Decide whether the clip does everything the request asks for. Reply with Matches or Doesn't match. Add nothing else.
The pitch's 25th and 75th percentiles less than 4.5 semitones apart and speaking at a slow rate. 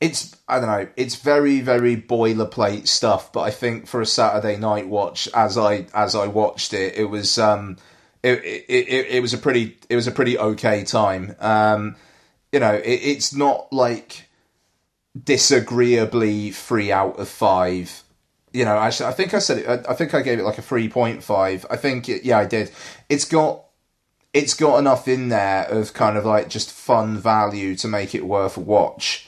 Doesn't match